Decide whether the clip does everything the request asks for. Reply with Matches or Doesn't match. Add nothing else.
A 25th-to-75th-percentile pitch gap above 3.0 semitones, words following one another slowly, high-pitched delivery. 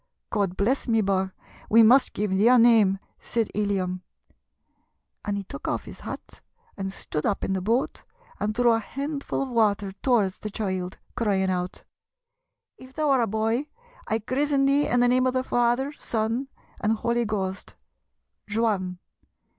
Doesn't match